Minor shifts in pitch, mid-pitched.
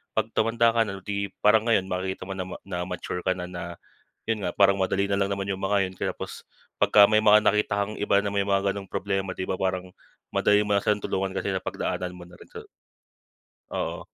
No: narrow, 1.7 semitones; low, 100 Hz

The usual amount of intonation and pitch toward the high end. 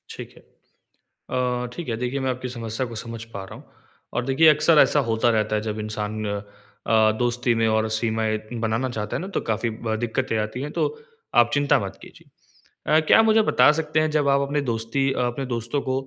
No: average, 3.9 semitones; low, 120 Hz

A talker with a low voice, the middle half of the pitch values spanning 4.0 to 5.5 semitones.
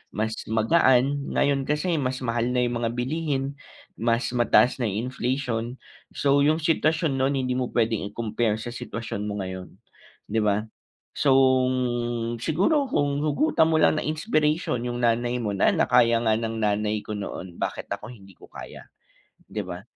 Yes: low, 120 Hz; average, 4.4 semitones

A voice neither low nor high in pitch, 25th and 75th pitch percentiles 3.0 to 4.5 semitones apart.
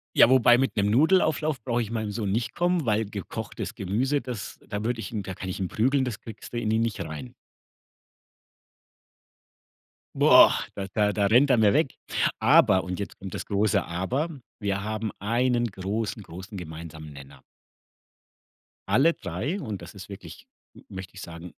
No: low, 105 Hz; average, 4.2 semitones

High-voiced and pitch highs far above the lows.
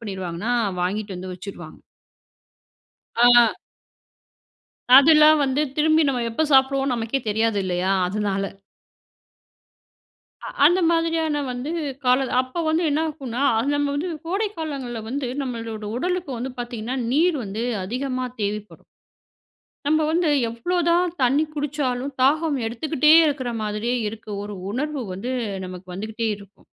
Yes: very high, 255 Hz; wide, 5.9 semitones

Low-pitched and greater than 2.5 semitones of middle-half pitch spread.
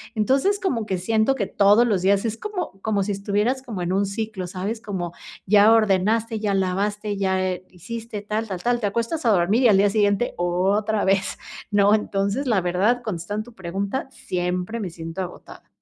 No: high, 205 Hz; average, 2.9 semitones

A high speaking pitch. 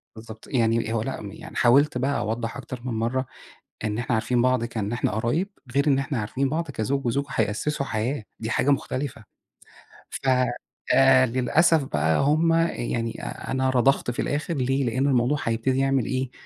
No: low, 130 Hz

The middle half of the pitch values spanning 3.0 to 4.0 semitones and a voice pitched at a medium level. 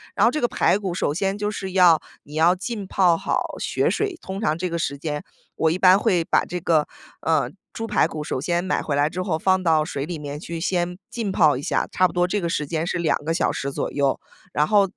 Yes: average, 3.4 semitones; medium, 175 Hz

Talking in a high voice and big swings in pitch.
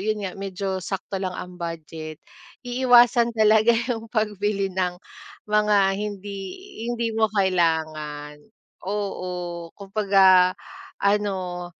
No: high, 195 Hz; average, 2.8 semitones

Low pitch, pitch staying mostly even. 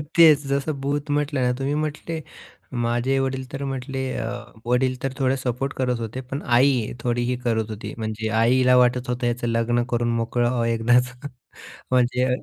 Yes: low, 125 Hz; narrow, 2.1 semitones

